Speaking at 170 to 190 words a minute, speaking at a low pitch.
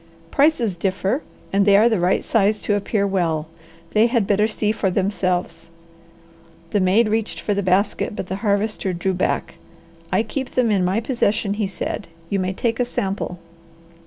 No: average, 175 wpm; high, 200 Hz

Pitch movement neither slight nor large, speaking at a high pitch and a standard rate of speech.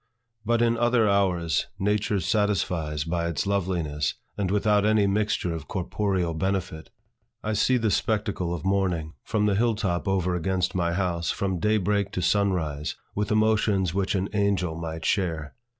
No: average, 3.4 semitones; very low, 95 Hz; average, 165 wpm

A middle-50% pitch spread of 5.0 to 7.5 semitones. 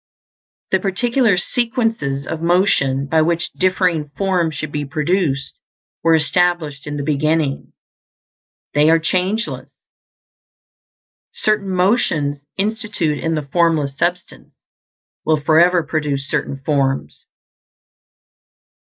No: average, 4.0 semitones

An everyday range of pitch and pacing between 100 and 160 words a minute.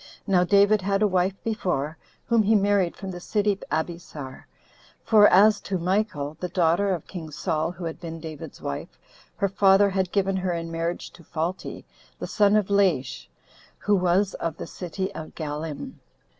No: average, 3.4 semitones; average, 170 wpm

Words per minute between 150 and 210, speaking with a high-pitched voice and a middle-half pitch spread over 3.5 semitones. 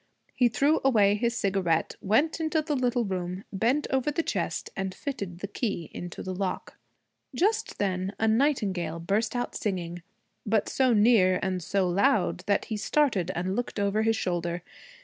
Yes: average, 170 wpm; high, 205 Hz; average, 5.0 semitones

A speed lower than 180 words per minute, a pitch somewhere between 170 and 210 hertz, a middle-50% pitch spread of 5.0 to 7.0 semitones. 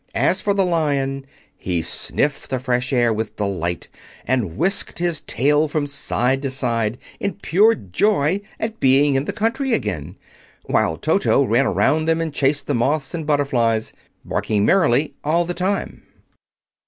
No: average, 155 wpm; medium, 140 Hz; wide, 5.5 semitones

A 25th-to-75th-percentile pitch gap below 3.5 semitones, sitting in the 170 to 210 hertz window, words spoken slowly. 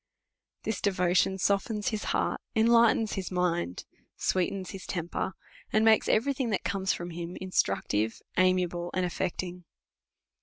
Yes: average, 3.1 semitones; medium, 185 Hz; slow, 130 wpm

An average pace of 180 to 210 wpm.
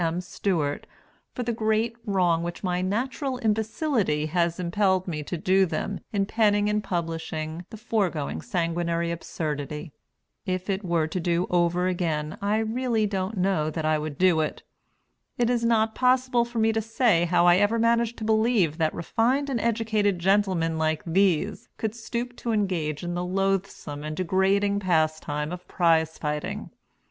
No: average, 165 wpm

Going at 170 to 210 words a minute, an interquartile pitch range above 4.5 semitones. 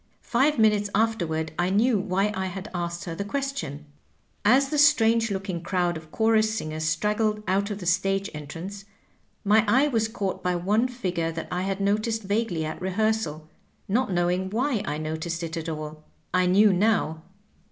No: average, 175 wpm; average, 4.2 semitones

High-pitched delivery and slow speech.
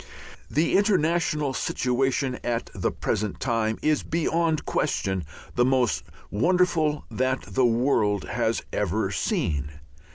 No: low, 130 Hz; slow, 110 wpm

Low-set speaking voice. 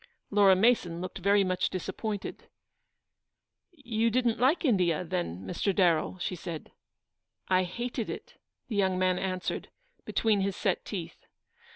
No: high, 190 Hz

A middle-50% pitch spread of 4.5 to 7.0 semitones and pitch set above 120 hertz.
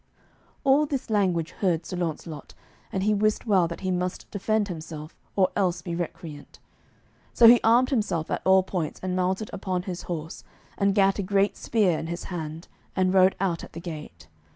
No: average, 3.2 semitones; medium, 185 Hz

